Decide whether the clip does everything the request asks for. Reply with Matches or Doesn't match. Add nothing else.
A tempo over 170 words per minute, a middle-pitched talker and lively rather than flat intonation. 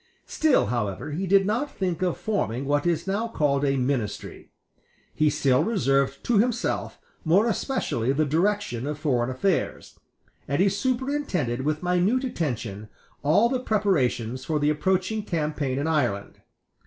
Doesn't match